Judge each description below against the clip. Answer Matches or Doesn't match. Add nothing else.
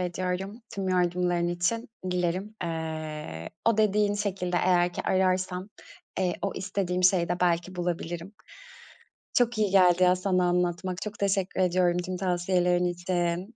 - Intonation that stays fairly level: Matches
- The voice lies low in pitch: Doesn't match